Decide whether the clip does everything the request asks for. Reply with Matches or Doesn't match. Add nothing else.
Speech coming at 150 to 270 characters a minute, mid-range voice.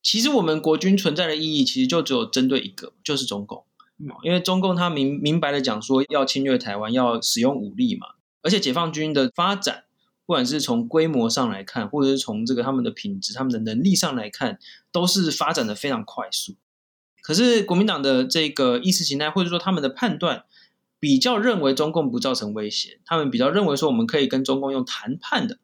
Doesn't match